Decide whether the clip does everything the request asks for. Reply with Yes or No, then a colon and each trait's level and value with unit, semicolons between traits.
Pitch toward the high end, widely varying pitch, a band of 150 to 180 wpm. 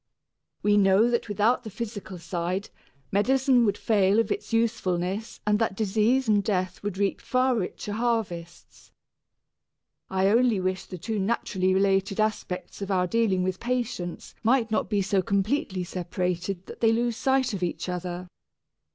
No: high, 205 Hz; average, 3.5 semitones; average, 155 wpm